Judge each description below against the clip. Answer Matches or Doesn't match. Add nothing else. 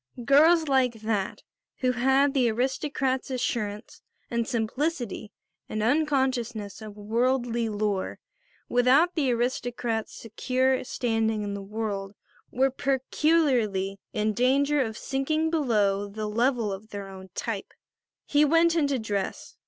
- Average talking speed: Doesn't match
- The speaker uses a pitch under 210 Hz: Doesn't match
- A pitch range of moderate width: Matches